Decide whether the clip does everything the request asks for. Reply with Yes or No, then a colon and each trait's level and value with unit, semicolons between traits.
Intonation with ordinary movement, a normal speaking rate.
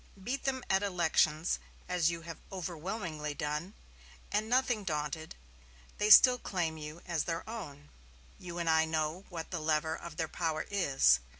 Yes: average, 3.6 semitones; average, 160 wpm